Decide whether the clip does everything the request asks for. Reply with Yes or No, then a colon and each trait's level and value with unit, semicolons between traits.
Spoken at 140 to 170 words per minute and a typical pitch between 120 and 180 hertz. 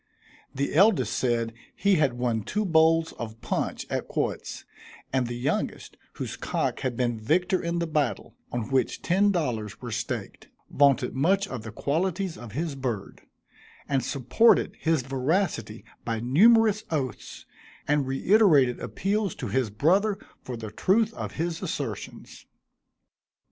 Yes: average, 145 wpm; medium, 140 Hz